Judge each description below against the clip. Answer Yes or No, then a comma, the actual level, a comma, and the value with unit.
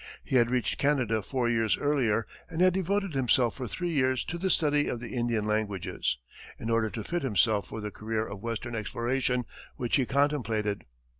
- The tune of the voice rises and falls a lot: No, average, 4.3 semitones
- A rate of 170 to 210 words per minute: Yes, average, 190 wpm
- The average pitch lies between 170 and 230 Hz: No, low, 120 Hz